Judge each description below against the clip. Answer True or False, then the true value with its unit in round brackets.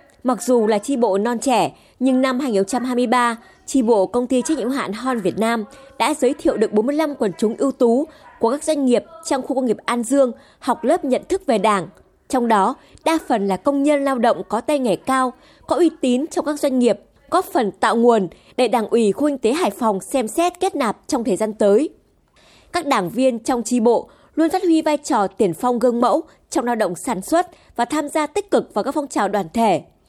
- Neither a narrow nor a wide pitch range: True (4.2 semitones)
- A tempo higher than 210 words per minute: True (230 wpm)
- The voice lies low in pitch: False (255 Hz)